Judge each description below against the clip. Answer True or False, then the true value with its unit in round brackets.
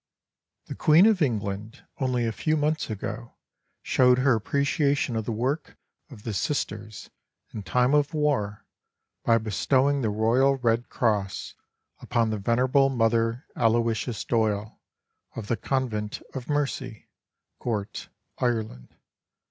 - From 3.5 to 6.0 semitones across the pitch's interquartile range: True (3.8 semitones)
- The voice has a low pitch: True (120 Hz)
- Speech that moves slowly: True (125 wpm)